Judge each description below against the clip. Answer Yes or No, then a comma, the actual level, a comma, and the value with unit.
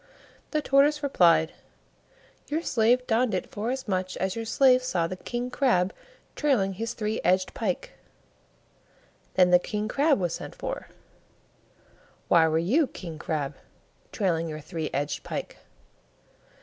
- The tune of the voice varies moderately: No, wide, 6.4 semitones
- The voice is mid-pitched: No, high, 200 Hz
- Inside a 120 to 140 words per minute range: Yes, slow, 135 wpm